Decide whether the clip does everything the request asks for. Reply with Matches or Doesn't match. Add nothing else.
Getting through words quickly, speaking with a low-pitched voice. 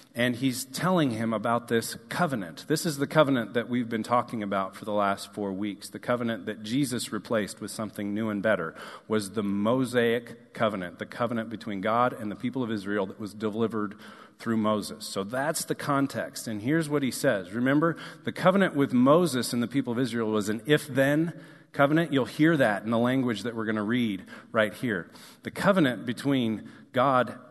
Doesn't match